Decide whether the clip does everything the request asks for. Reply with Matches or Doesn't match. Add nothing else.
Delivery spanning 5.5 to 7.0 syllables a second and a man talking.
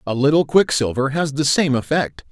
Doesn't match